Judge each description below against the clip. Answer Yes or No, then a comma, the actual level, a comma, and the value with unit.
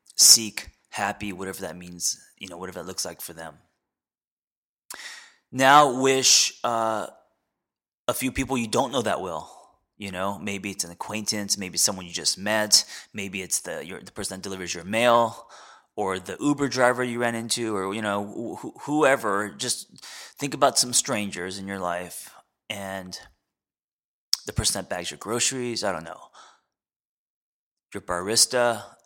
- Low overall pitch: Yes, low, 105 Hz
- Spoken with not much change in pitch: No, average, 3.7 semitones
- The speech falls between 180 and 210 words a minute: No, average, 160 wpm